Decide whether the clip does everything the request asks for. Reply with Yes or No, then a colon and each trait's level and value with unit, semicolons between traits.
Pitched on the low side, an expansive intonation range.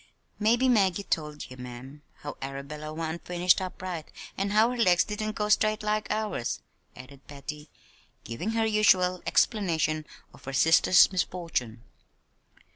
No: medium, 175 Hz; wide, 6.1 semitones